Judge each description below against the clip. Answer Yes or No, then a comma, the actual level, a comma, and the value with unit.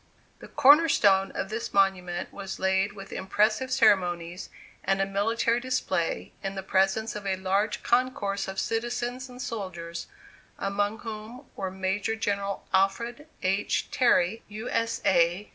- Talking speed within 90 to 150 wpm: Yes, average, 145 wpm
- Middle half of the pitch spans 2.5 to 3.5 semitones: Yes, average, 3.1 semitones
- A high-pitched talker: Yes, high, 200 Hz